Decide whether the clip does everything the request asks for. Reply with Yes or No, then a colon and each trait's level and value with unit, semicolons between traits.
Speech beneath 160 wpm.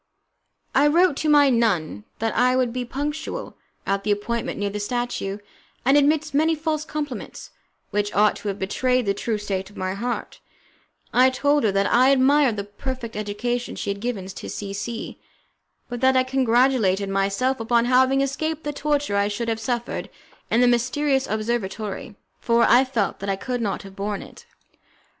No: average, 180 wpm